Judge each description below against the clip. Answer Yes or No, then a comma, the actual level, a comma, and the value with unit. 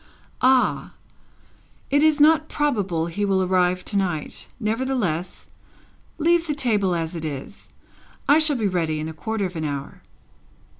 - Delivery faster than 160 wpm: No, average, 150 wpm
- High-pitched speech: Yes, high, 195 Hz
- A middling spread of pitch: No, wide, 8.2 semitones